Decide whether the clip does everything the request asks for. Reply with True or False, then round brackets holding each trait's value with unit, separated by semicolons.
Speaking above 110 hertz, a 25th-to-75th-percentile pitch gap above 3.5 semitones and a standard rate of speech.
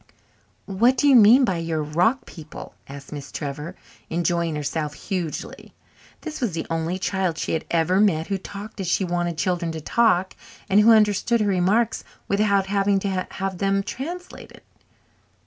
True (190 Hz; 4.0 semitones; 165 wpm)